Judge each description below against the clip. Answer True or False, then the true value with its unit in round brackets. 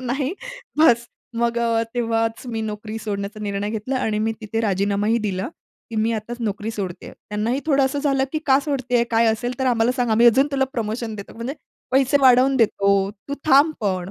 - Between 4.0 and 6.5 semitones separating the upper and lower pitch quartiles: False (3.3 semitones)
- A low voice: False (230 Hz)